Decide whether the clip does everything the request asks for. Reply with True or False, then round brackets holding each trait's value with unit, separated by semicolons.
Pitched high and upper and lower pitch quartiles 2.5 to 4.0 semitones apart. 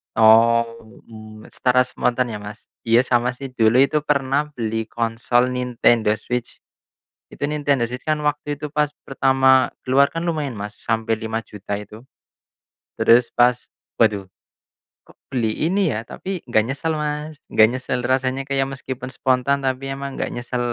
False (125 Hz; 3.4 semitones)